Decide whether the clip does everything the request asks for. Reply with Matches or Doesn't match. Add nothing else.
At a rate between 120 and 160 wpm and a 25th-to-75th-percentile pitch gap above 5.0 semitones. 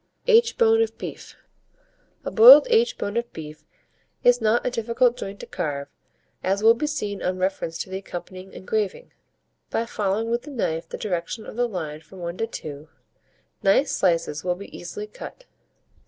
Doesn't match